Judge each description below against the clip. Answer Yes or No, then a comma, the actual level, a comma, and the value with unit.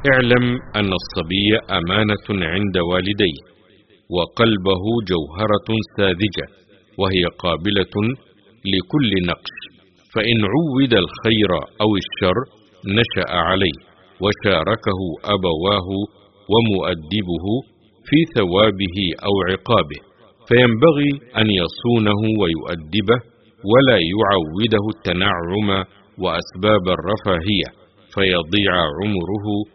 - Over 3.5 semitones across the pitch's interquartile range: No, average, 2.8 semitones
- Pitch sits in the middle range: No, low, 105 Hz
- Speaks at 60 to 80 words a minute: Yes, average, 75 wpm